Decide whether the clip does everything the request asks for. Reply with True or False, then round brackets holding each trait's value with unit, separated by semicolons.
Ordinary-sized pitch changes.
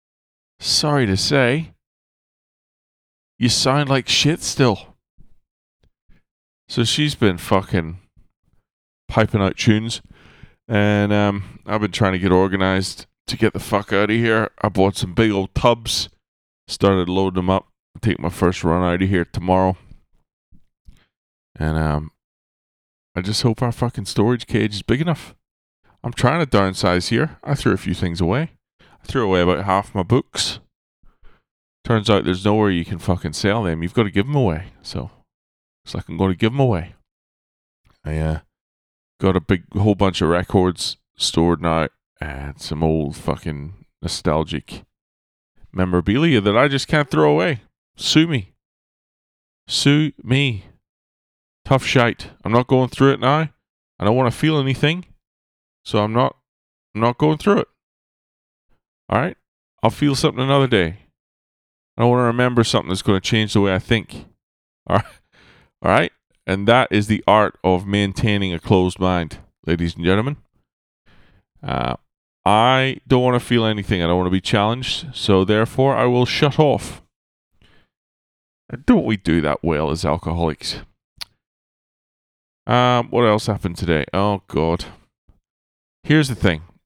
False (6.0 semitones)